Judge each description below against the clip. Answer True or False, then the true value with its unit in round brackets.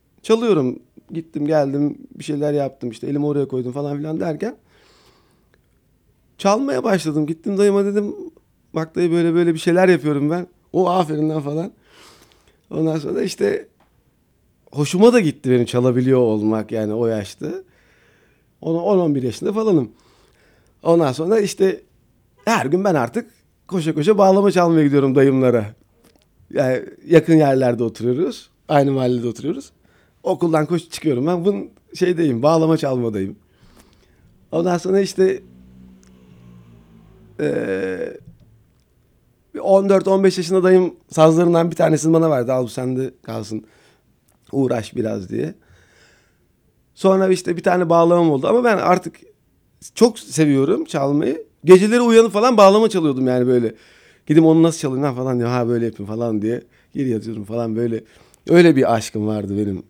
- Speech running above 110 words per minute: True (135 wpm)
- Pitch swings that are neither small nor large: False (6.7 semitones)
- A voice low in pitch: False (155 Hz)